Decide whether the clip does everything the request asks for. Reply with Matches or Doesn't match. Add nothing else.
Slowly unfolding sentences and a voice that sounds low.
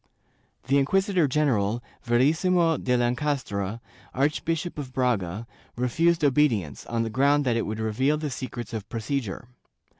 Matches